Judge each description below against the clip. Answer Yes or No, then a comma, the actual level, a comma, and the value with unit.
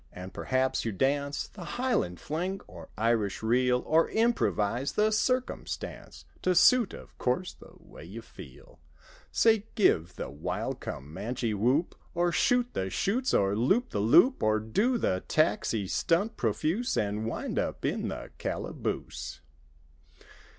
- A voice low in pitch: Yes, low, 130 Hz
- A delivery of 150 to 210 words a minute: No, average, 140 wpm